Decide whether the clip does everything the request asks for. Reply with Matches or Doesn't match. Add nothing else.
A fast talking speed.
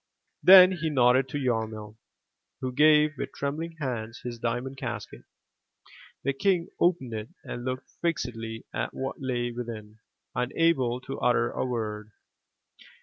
Doesn't match